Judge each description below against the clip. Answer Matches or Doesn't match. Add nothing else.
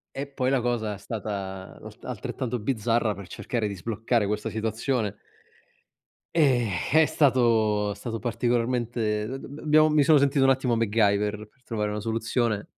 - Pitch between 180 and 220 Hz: Doesn't match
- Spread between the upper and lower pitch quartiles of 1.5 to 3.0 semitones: Doesn't match